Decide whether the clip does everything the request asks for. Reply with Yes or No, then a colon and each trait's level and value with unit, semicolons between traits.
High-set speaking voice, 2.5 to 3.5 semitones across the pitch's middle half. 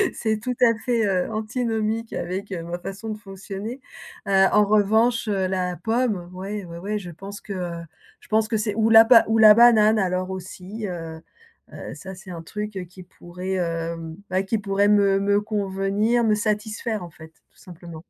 Yes: high, 200 Hz; average, 2.9 semitones